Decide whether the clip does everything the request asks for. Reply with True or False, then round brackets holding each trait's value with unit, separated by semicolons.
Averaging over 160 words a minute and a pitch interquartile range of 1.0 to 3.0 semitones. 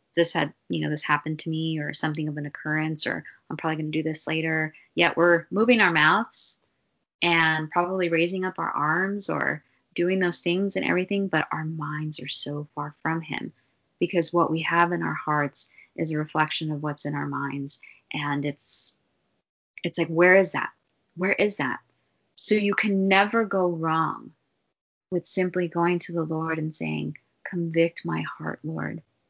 True (180 wpm; 2.5 semitones)